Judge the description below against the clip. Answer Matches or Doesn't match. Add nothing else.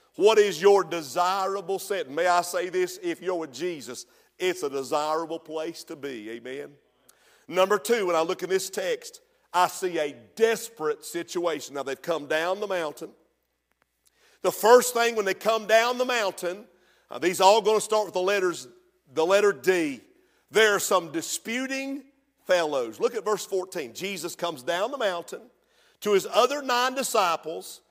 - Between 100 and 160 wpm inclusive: Doesn't match